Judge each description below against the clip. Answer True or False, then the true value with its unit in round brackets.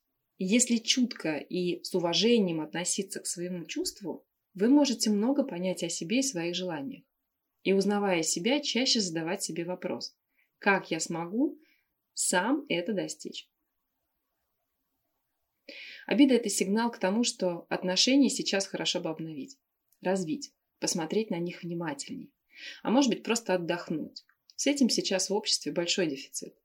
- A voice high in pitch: True (200 Hz)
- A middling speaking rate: True (135 wpm)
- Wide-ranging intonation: True (6.2 semitones)